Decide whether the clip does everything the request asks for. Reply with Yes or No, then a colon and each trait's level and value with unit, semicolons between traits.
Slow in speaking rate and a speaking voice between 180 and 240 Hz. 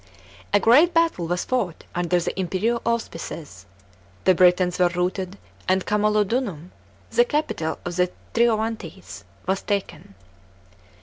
Yes: slow, 125 wpm; high, 190 Hz